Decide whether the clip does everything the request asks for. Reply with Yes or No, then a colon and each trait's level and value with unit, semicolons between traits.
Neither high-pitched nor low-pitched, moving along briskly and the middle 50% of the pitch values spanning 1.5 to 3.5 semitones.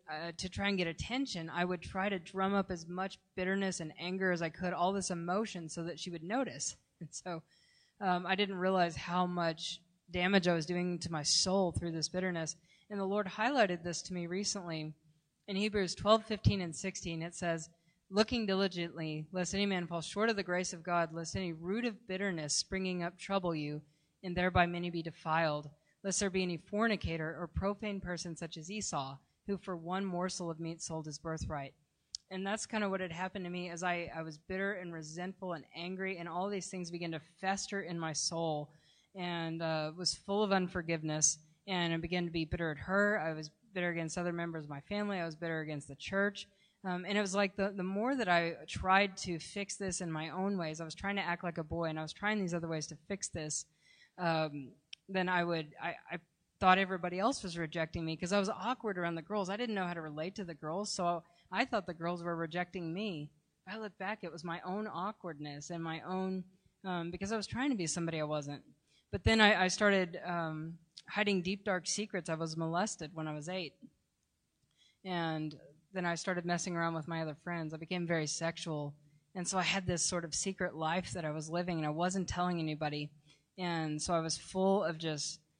Yes: medium, 175 Hz; fast, 220 wpm; average, 2.8 semitones